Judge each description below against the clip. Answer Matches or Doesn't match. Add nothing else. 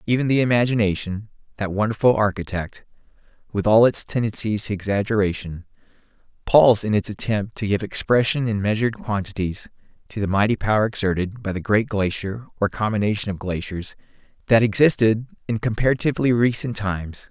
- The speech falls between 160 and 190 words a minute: Doesn't match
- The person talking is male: Matches